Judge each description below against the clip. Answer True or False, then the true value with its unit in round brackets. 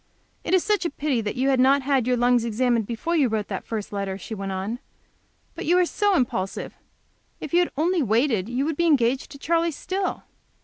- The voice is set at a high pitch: True (260 Hz)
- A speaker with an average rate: False (215 wpm)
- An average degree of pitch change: False (6.4 semitones)